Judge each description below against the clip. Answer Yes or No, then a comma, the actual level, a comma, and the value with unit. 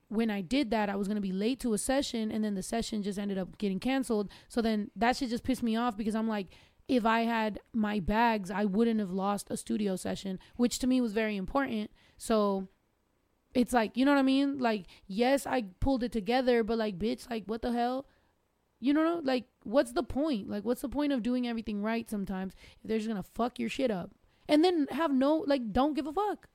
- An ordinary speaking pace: No, fast, 235 wpm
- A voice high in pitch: Yes, high, 230 Hz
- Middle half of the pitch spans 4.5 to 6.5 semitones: No, average, 3.7 semitones